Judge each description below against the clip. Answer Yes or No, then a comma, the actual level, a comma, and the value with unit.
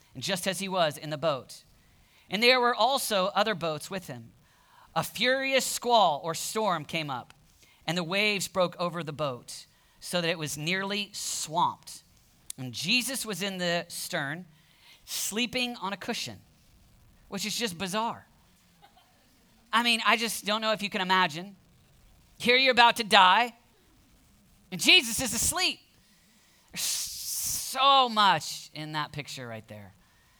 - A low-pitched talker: No, high, 190 Hz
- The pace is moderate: Yes, average, 150 wpm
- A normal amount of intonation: No, wide, 6.1 semitones